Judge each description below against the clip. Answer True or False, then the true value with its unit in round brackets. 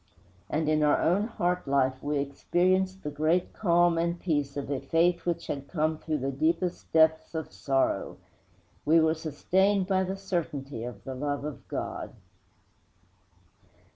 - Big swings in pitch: False (3.6 semitones)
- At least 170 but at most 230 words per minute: False (155 wpm)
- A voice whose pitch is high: False (160 Hz)